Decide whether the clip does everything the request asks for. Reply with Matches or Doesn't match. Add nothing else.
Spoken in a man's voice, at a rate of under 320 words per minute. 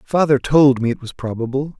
Matches